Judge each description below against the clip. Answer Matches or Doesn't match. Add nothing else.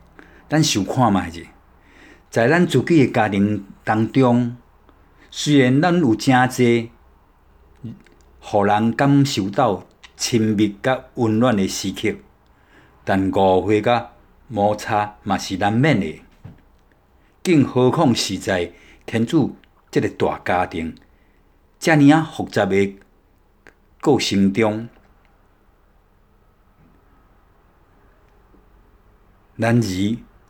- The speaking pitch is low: Matches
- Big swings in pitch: Doesn't match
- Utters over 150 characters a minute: Doesn't match